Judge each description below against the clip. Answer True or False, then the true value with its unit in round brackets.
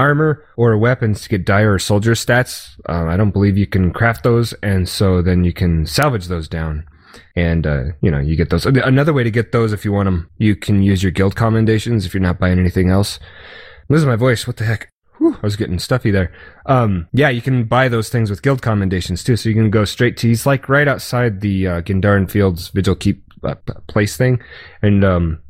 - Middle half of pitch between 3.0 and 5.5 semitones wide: True (4.6 semitones)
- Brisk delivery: True (230 wpm)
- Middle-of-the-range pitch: False (105 Hz)